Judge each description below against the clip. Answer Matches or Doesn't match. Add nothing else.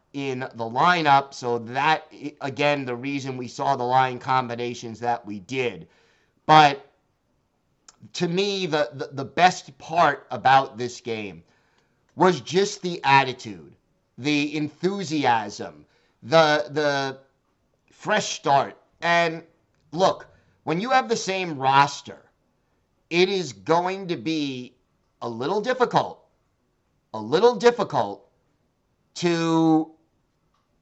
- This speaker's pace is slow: Matches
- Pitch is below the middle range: Doesn't match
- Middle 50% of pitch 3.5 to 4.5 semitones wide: Doesn't match